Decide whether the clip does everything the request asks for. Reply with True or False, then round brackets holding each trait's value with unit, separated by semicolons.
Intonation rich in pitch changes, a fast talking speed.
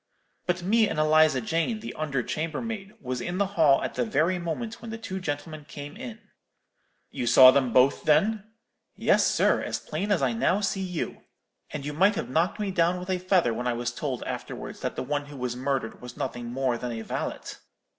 True (6.6 semitones; 210 wpm)